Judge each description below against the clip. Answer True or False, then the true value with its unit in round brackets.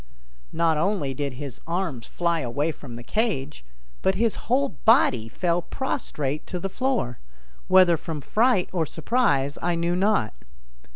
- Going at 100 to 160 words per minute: True (150 wpm)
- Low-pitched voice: False (170 Hz)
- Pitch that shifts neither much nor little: False (5.9 semitones)